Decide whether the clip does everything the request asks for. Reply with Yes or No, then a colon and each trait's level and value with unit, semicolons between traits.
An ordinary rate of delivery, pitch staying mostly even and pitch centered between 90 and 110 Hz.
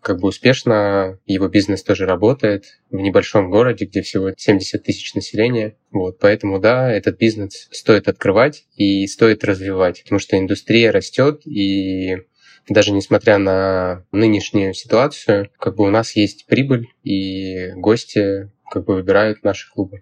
Yes: average, 145 wpm; narrow, 1.9 semitones; low, 100 Hz